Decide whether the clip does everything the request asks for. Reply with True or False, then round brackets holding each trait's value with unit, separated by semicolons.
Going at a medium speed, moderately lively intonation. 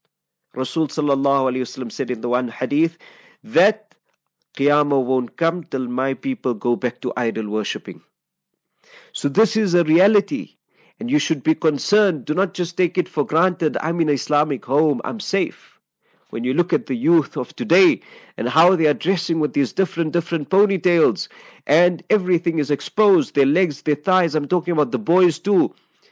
True (170 wpm; 4.6 semitones)